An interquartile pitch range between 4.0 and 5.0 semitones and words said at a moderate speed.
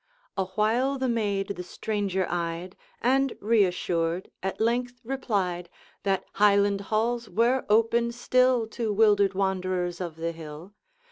No: average, 4.3 semitones; slow, 125 wpm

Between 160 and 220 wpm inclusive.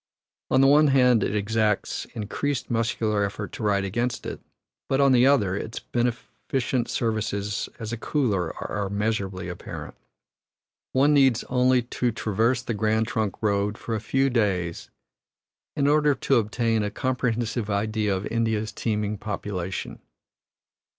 No: average, 145 wpm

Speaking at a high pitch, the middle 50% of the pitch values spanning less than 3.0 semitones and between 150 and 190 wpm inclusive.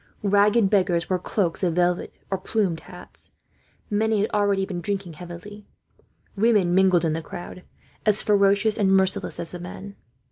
Yes: high, 195 Hz; narrow, 2.5 semitones; average, 155 wpm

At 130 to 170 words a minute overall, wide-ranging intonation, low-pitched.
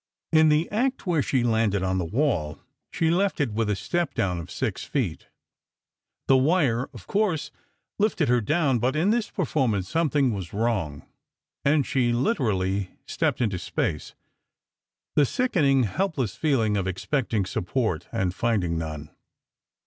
Yes: average, 150 wpm; wide, 7.9 semitones; low, 120 Hz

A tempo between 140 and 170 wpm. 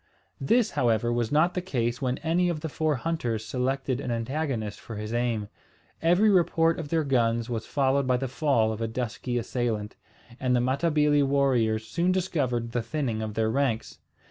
No: average, 180 wpm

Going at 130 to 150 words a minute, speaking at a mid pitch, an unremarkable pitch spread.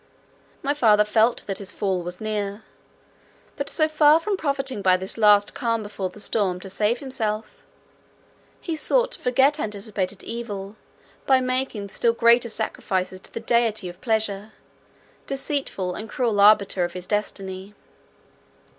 No: average, 145 wpm; high, 215 Hz; average, 4.2 semitones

